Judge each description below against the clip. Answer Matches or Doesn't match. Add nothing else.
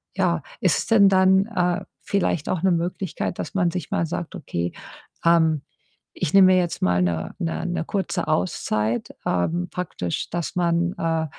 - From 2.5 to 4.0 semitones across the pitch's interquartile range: Matches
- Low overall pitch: Doesn't match